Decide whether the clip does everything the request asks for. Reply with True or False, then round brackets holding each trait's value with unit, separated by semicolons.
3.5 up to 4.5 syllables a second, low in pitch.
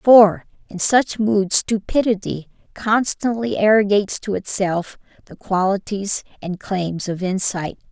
False (4.0 syllables/s; 200 Hz)